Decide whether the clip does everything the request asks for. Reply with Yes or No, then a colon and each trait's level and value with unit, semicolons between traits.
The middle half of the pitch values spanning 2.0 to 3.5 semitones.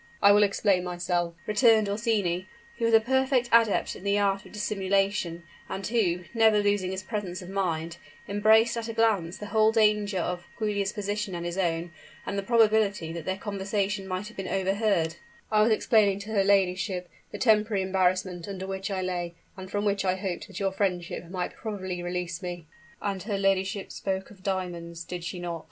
Yes: narrow, 2.6 semitones